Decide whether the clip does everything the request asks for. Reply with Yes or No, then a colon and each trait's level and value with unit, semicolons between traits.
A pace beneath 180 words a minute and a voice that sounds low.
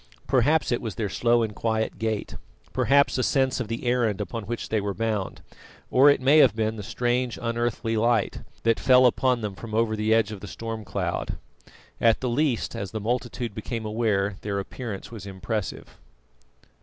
No: average, 185 wpm; low, 115 Hz